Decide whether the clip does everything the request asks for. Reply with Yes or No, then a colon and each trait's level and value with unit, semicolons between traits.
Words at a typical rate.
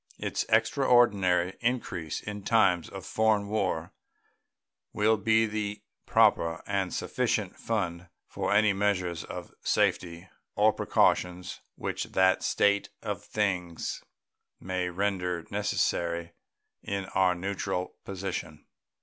No: slow, 105 wpm